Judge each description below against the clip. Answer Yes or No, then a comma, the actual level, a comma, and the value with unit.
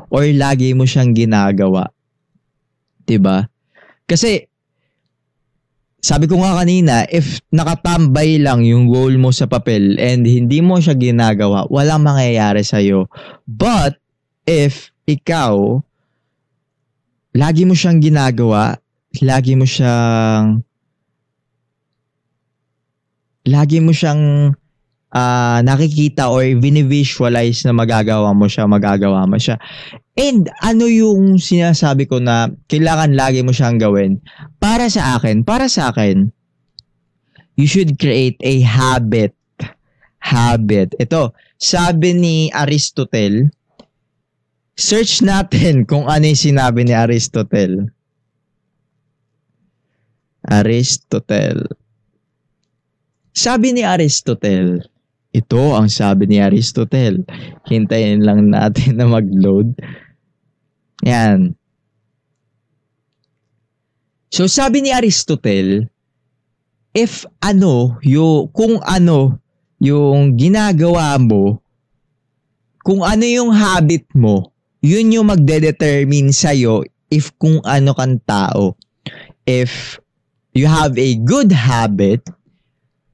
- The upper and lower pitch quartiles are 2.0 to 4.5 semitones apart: No, average, 5.3 semitones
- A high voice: No, low, 135 Hz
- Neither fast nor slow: No, slow, 95 wpm